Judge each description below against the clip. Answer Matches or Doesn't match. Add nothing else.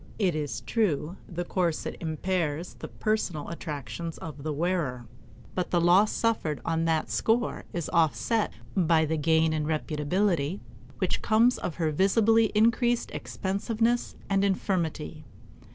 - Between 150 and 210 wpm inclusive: Doesn't match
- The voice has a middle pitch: Matches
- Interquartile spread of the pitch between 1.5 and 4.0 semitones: Doesn't match